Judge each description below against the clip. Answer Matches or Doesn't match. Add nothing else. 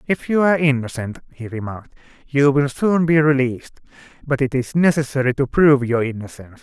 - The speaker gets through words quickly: Doesn't match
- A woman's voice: Doesn't match